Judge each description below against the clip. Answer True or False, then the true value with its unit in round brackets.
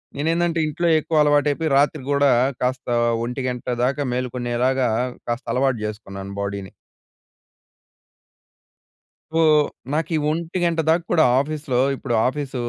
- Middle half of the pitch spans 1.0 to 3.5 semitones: False (4.1 semitones)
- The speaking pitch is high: False (140 Hz)